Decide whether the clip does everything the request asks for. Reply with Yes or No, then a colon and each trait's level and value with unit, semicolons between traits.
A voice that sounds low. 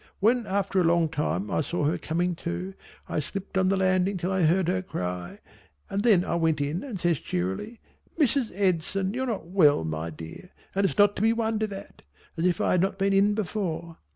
No: medium, 185 Hz